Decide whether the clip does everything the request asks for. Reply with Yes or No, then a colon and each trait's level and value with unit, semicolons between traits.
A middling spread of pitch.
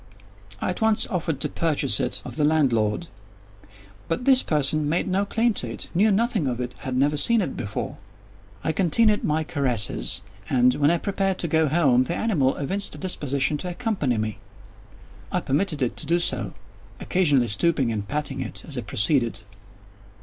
No: wide, 6.2 semitones